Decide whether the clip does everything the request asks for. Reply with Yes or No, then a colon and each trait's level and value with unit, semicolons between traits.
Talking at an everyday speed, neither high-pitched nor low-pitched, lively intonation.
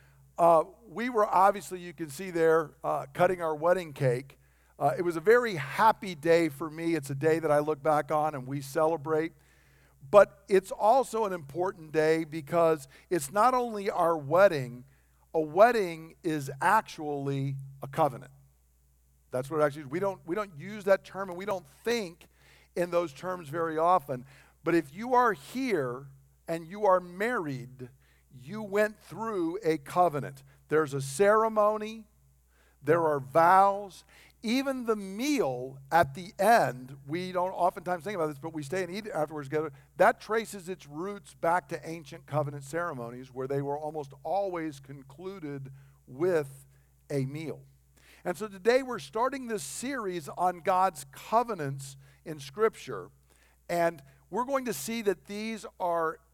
Yes: average, 160 wpm; medium, 165 Hz; wide, 5.7 semitones